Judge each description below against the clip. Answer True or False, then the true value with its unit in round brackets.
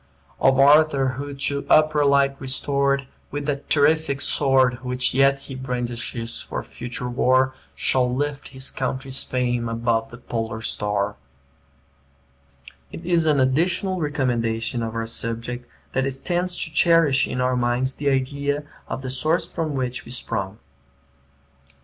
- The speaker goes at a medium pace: True (150 wpm)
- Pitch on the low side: True (130 Hz)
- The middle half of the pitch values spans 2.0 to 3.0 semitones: True (2.7 semitones)